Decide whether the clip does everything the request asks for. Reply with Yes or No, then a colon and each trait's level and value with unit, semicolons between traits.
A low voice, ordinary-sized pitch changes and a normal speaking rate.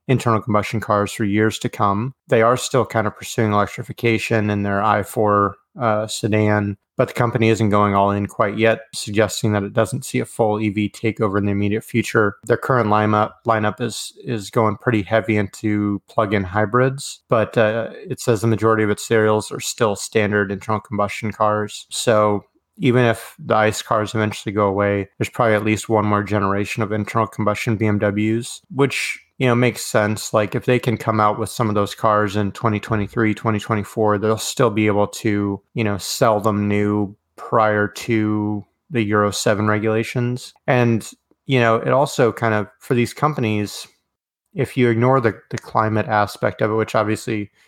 No: low, 110 Hz; narrow, 1.6 semitones; average, 180 wpm